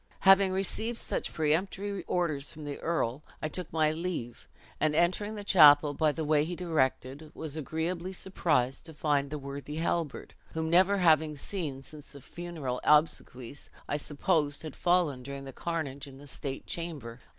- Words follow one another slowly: No, average, 165 wpm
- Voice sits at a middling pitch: Yes, medium, 155 Hz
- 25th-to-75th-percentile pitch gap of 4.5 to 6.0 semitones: No, average, 3.4 semitones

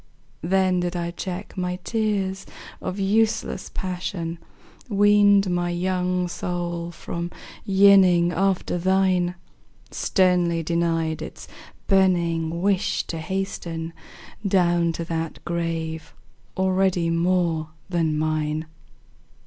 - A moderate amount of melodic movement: No, narrow, 2.2 semitones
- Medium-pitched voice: Yes, medium, 175 Hz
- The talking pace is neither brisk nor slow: No, slow, 100 wpm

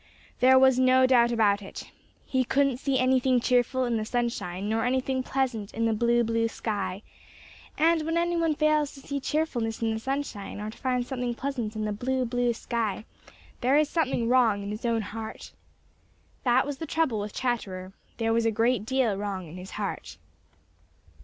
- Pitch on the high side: Yes, high, 240 Hz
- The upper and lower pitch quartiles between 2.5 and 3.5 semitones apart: Yes, average, 3.1 semitones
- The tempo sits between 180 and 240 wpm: Yes, average, 185 wpm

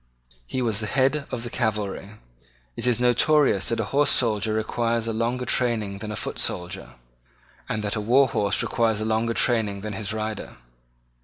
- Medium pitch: No, low, 110 Hz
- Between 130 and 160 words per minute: No, average, 185 wpm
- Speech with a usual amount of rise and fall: No, narrow, 2.3 semitones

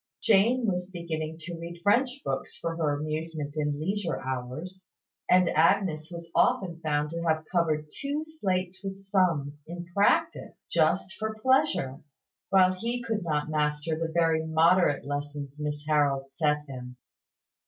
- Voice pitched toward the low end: No, medium, 165 Hz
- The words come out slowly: No, average, 145 wpm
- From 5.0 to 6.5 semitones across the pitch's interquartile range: No, average, 4.3 semitones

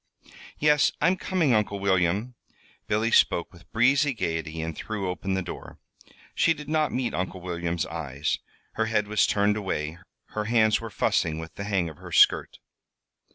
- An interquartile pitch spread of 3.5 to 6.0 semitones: Yes, average, 5.1 semitones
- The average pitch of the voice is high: No, low, 100 Hz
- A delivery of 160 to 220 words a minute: Yes, average, 170 wpm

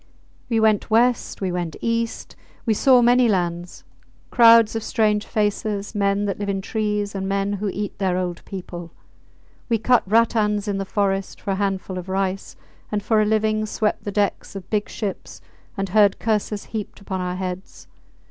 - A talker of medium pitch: No, high, 205 Hz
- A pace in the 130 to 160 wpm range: No, average, 175 wpm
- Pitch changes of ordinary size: No, narrow, 2.1 semitones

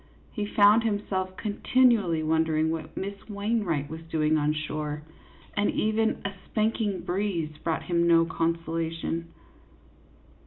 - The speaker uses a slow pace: Yes, slow, 125 wpm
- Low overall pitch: No, medium, 170 Hz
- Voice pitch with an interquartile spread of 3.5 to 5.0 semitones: Yes, average, 4.3 semitones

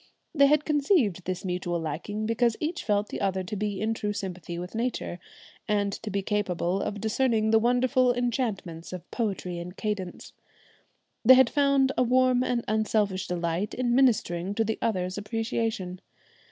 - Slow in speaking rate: No, average, 165 wpm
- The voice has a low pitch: No, high, 210 Hz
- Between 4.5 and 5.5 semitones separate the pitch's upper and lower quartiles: Yes, average, 4.8 semitones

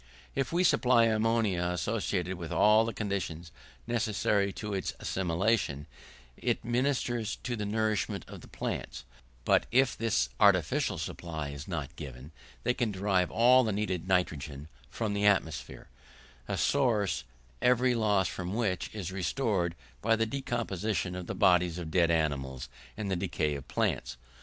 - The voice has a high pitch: No, low, 100 Hz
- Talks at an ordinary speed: Yes, average, 150 wpm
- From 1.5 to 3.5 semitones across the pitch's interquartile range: No, average, 4.8 semitones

